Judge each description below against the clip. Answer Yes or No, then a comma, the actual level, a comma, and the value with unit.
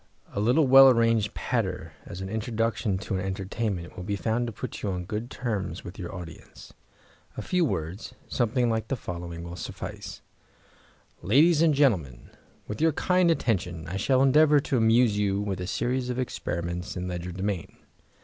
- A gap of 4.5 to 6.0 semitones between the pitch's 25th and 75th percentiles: Yes, average, 5.3 semitones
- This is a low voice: Yes, low, 105 Hz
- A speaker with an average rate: Yes, average, 170 wpm